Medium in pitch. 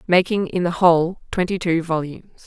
Yes: medium, 175 Hz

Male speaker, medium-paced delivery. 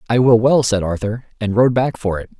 No: male; fast, 250 wpm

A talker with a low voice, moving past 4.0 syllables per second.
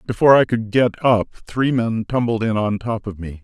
Yes: low, 115 Hz; 5.4 syllables/s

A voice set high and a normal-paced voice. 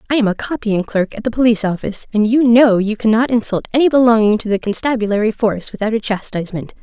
No: high, 220 Hz; fast, 210 wpm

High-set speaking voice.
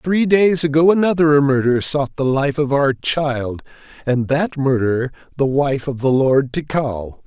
No: medium, 140 Hz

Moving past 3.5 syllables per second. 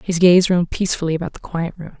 Yes: 6.8 syllables/s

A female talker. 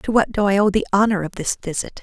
Yes: female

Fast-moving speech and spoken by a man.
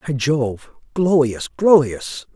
No: slow, 100 wpm; male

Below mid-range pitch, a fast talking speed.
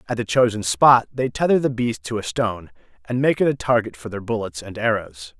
Yes: low, 110 Hz; fast, 235 wpm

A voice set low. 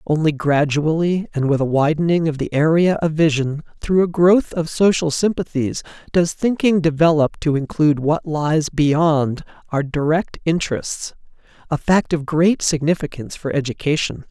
No: medium, 155 Hz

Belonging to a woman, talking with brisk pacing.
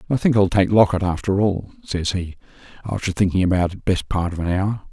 No: male; fast, 220 wpm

